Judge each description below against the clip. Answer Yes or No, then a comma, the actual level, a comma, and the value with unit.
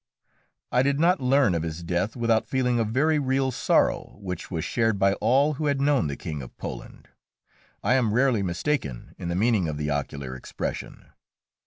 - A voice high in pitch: No, low, 115 Hz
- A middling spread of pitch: No, wide, 7.6 semitones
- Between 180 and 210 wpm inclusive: Yes, average, 185 wpm